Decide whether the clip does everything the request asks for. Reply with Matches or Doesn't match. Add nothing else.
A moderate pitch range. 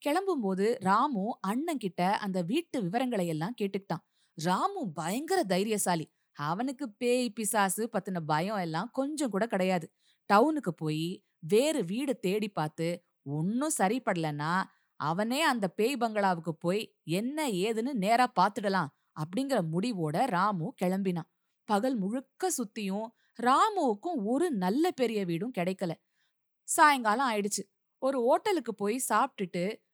Doesn't match